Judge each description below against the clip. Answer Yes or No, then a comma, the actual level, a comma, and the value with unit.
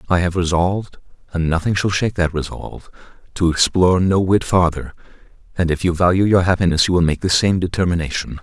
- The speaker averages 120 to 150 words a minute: No, average, 185 wpm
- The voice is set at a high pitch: No, very low, 90 Hz